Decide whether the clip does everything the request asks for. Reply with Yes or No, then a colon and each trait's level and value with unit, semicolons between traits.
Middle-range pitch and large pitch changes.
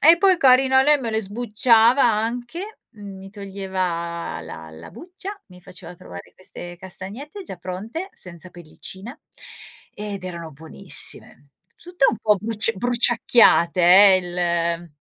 No: high, 200 Hz; wide, 5.8 semitones